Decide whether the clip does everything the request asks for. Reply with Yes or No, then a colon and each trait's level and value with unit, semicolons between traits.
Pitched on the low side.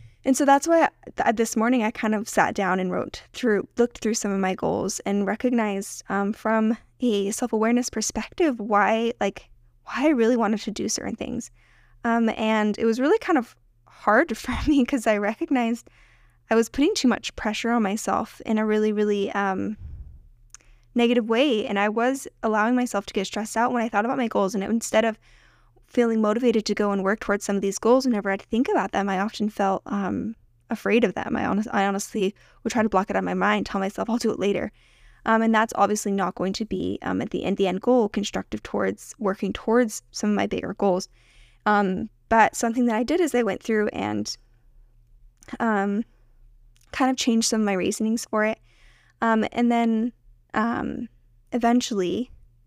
No: high, 215 Hz